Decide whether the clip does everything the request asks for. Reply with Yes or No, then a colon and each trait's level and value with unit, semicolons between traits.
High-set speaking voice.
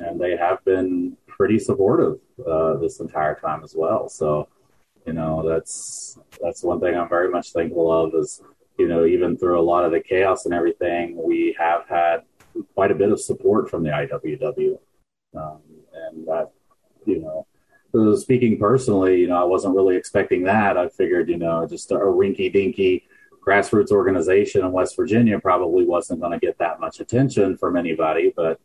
No: low, 105 Hz